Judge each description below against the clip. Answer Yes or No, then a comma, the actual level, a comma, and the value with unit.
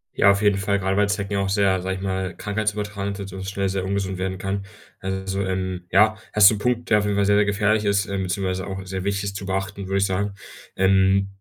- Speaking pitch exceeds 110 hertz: No, low, 100 Hz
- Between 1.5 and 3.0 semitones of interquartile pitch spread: No, narrow, 1.1 semitones